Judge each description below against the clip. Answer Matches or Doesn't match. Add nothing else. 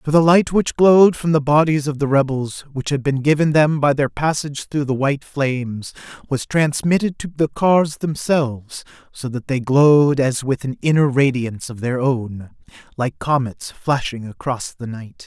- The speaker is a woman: Doesn't match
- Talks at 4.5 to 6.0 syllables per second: Matches